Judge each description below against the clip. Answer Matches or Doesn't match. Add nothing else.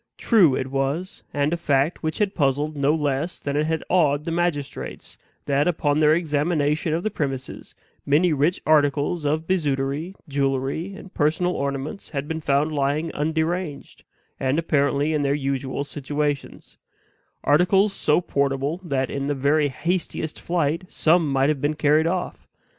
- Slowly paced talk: Doesn't match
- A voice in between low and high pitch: Matches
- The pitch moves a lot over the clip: Doesn't match